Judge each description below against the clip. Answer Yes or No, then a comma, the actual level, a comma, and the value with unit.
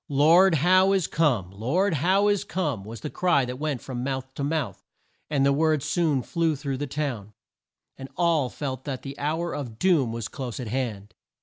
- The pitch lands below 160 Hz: Yes, medium, 140 Hz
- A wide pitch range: No, average, 4.4 semitones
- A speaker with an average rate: Yes, average, 195 wpm